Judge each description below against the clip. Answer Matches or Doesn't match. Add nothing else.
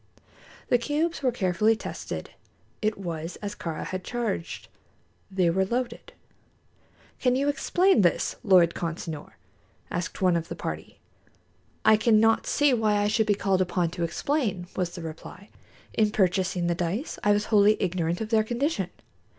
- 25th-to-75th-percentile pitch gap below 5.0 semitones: Matches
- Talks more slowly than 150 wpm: Doesn't match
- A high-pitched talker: Matches